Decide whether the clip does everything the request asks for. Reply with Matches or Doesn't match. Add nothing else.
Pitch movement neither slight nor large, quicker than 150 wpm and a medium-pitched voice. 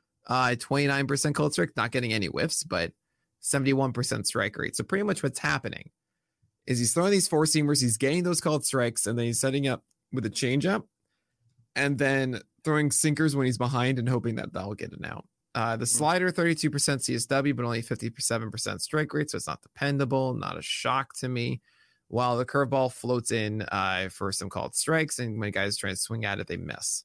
Doesn't match